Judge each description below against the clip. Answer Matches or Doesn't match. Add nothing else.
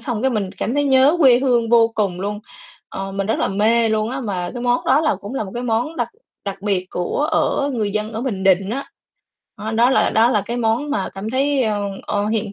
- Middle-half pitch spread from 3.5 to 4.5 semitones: Matches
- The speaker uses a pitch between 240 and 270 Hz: Doesn't match